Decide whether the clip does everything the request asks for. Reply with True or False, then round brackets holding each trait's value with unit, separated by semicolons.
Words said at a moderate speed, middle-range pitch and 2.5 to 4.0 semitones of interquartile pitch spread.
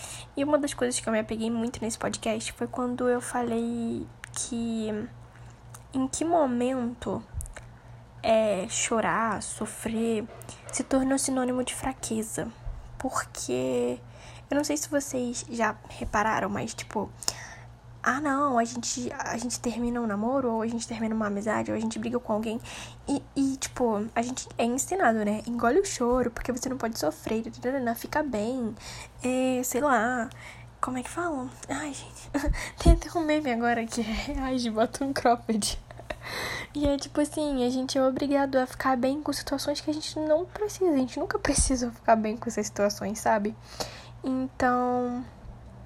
False (165 wpm; 245 Hz; 3.3 semitones)